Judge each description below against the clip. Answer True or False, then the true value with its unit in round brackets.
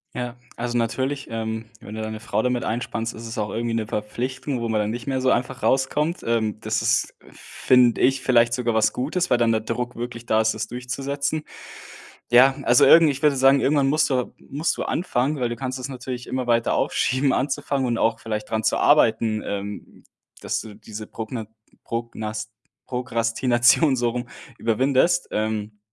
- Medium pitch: False (120 Hz)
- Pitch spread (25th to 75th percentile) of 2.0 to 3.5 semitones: True (2.8 semitones)